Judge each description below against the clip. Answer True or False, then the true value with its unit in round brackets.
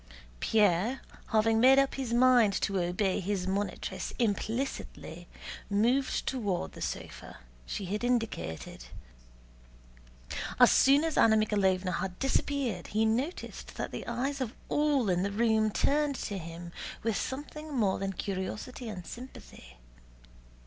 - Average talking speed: False (130 wpm)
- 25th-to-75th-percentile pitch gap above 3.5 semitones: True (5.1 semitones)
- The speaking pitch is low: False (220 Hz)